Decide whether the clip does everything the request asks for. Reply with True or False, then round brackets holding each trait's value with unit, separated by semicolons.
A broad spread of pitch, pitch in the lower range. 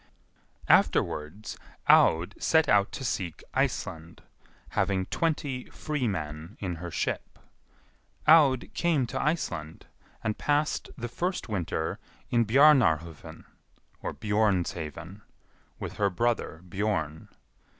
True (8.0 semitones; 105 Hz)